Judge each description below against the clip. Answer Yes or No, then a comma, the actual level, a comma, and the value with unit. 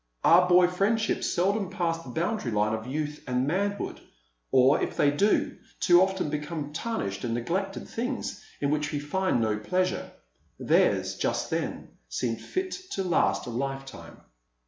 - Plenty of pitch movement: Yes, wide, 5.9 semitones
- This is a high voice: No, medium, 165 Hz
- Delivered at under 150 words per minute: No, average, 155 wpm